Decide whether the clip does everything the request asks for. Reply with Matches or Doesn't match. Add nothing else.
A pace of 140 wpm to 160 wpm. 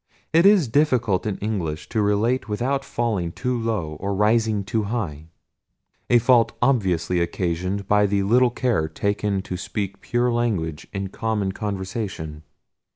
Matches